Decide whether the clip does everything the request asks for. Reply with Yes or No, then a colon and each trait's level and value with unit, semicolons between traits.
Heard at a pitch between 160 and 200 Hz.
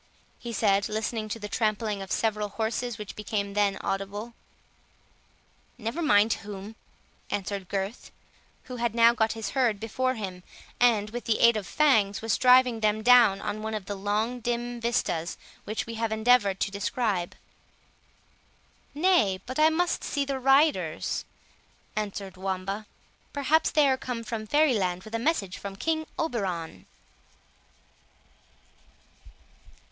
No: high, 220 Hz